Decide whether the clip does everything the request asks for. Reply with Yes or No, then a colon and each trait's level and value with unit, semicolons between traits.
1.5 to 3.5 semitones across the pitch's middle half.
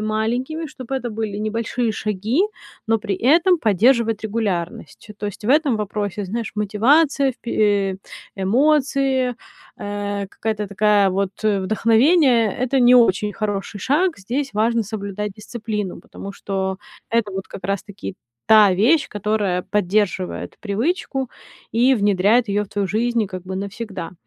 Yes: average, 3.2 semitones